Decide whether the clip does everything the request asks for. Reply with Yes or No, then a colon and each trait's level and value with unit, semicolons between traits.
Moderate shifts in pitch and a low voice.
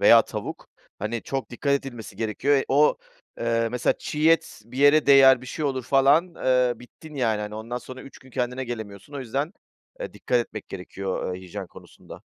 Yes: average, 3.8 semitones; low, 125 Hz